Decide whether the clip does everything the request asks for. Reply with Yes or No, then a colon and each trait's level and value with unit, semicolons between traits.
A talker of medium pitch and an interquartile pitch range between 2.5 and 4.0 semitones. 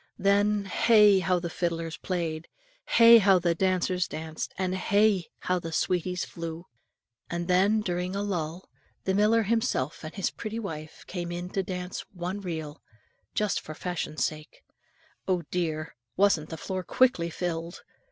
Yes: medium, 180 Hz; average, 2.9 semitones